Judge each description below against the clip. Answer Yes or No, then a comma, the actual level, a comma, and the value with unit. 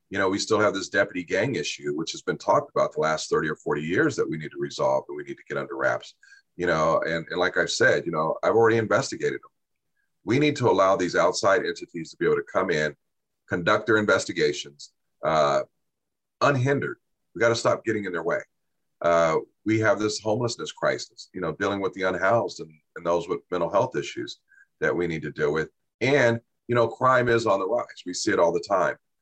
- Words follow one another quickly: Yes, fast, 225 wpm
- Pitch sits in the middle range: No, low, 120 Hz